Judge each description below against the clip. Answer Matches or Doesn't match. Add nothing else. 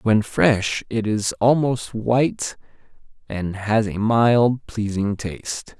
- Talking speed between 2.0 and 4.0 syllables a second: Matches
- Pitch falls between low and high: Doesn't match